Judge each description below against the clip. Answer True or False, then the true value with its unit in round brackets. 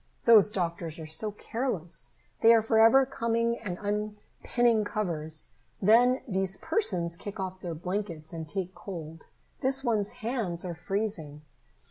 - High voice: True (200 Hz)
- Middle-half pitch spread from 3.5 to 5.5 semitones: True (5.0 semitones)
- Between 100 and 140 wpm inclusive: True (135 wpm)